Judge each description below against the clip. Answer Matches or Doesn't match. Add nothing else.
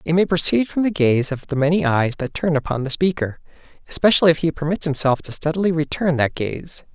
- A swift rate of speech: Matches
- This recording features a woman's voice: Doesn't match